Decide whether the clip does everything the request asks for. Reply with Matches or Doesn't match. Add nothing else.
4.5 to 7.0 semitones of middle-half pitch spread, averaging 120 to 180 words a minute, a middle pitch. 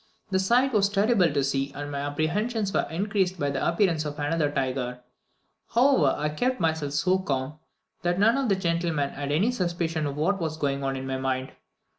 Doesn't match